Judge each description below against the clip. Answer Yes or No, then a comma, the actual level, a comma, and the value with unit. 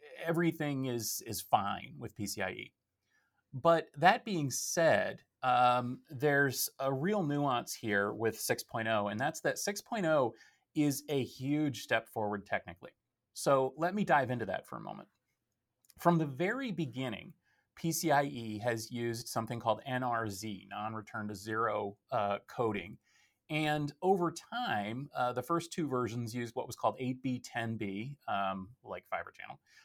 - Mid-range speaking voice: No, low, 125 Hz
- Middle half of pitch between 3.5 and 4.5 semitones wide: No, average, 5.1 semitones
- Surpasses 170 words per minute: No, average, 140 wpm